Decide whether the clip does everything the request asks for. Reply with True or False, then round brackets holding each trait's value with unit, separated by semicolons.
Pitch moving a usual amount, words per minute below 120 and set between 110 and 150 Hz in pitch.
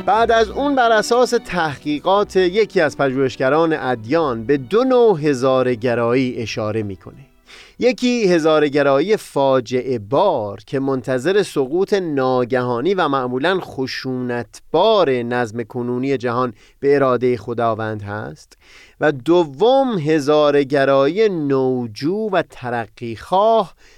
False (6.2 semitones; 105 wpm; 135 Hz)